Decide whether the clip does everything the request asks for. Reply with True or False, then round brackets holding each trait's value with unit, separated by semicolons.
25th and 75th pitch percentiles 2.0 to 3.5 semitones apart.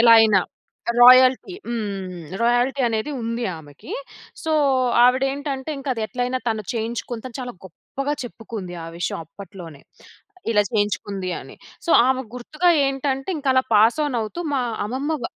False (4.0 semitones)